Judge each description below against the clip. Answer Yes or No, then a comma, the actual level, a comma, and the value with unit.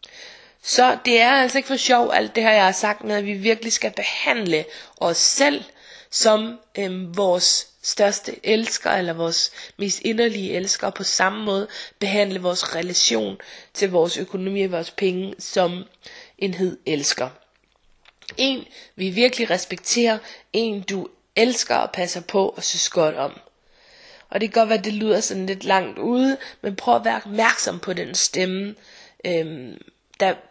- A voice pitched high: Yes, high, 200 Hz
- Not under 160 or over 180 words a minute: Yes, average, 165 wpm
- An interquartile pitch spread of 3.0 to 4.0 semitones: Yes, average, 3.5 semitones